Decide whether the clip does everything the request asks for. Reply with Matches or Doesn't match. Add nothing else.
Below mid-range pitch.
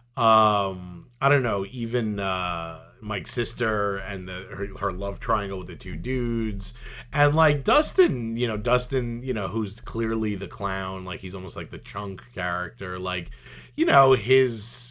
Matches